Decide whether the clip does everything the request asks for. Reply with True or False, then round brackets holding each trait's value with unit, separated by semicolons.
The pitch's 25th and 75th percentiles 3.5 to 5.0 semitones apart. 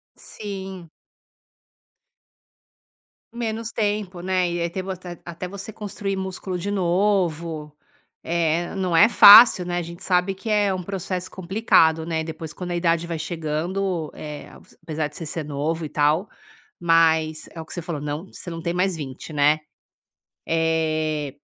False (3.1 semitones)